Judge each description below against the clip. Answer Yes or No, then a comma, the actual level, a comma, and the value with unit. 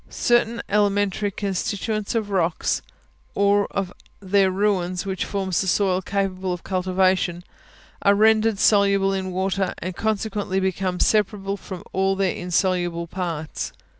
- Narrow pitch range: Yes, narrow, 1.7 semitones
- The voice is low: No, high, 195 Hz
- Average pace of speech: No, slow, 130 wpm